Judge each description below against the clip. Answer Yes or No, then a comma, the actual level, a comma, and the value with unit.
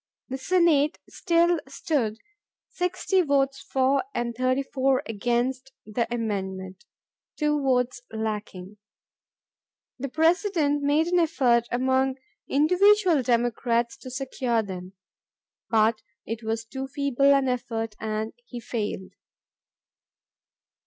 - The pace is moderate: No, slow, 100 wpm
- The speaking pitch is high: Yes, very high, 255 Hz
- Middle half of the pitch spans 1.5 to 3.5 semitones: No, average, 4.1 semitones